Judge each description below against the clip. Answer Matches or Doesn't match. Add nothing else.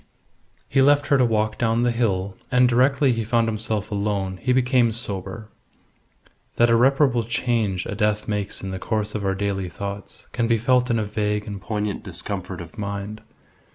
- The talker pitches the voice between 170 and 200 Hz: Doesn't match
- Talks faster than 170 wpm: Matches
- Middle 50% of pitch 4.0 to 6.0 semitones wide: Doesn't match